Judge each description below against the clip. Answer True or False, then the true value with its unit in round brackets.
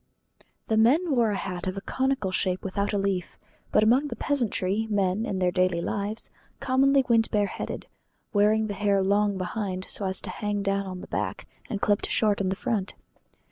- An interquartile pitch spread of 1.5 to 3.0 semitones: True (2.6 semitones)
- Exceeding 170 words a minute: True (190 wpm)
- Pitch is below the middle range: False (205 Hz)